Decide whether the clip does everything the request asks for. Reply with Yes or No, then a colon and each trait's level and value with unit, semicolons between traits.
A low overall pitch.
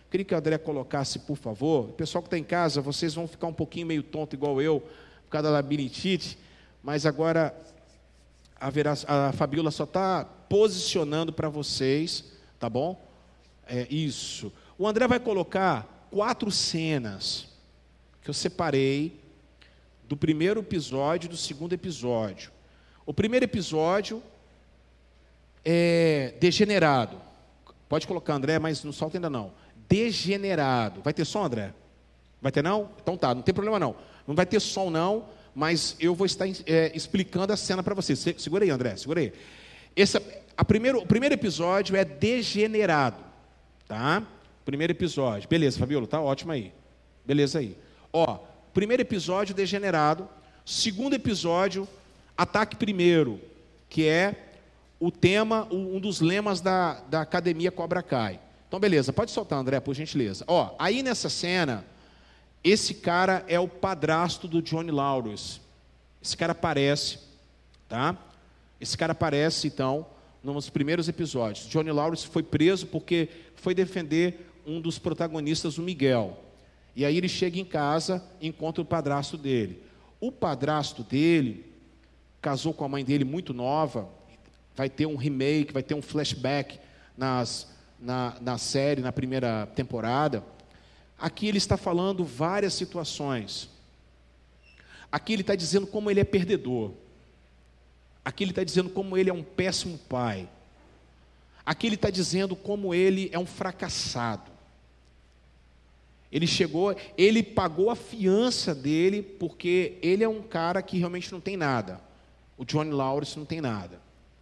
No: medium, 155 Hz